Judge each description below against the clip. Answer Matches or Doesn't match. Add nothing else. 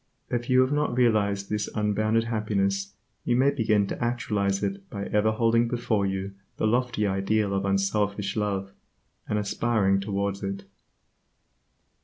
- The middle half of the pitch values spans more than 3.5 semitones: Doesn't match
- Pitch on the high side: Doesn't match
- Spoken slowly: Doesn't match